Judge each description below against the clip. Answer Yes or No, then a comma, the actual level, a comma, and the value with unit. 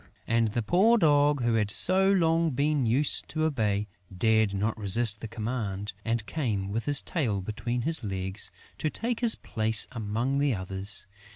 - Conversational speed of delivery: Yes, average, 170 wpm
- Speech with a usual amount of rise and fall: No, wide, 5.9 semitones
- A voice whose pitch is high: No, low, 115 Hz